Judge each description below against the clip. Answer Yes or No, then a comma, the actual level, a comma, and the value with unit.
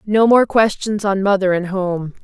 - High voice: Yes, high, 200 Hz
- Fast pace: No, average, 190 wpm